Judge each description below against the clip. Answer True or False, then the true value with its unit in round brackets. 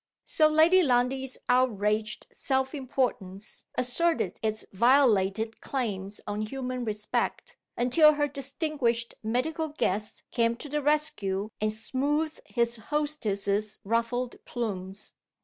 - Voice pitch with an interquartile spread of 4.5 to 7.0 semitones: True (4.8 semitones)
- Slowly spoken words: True (110 wpm)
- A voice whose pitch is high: True (245 Hz)